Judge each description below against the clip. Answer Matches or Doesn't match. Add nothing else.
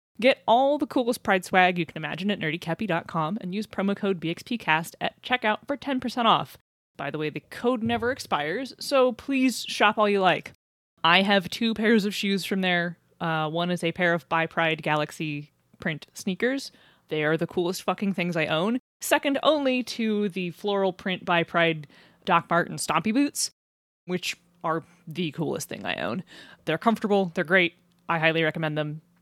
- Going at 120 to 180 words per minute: Matches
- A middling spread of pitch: Matches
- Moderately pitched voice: Matches